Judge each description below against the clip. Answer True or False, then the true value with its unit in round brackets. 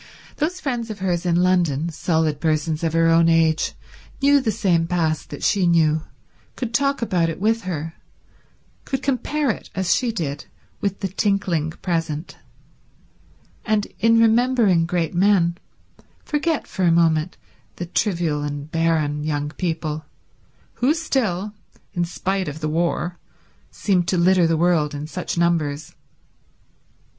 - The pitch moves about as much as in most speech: True (4.4 semitones)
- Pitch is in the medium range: True (175 Hz)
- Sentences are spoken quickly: False (145 wpm)